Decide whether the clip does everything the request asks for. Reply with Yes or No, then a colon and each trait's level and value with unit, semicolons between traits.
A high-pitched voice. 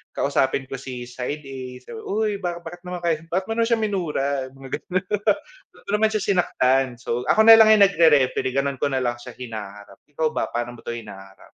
No: medium, 140 Hz